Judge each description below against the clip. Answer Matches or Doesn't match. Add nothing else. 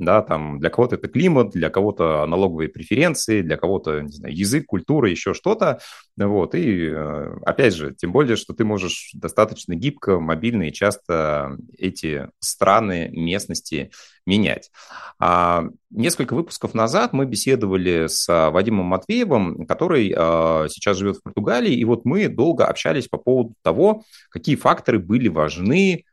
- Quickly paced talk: Doesn't match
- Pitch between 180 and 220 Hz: Doesn't match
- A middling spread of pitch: Doesn't match